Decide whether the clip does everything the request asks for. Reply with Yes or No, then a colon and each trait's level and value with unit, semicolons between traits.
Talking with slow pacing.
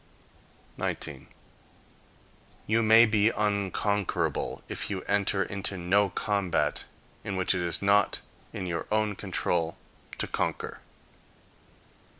Yes: slow, 110 wpm